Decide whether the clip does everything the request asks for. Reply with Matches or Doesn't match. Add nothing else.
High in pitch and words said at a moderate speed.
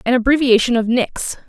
Matches